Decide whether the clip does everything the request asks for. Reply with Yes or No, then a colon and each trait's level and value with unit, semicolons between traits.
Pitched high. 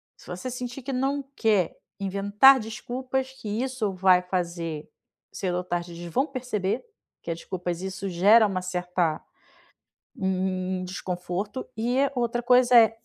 Yes: high, 200 Hz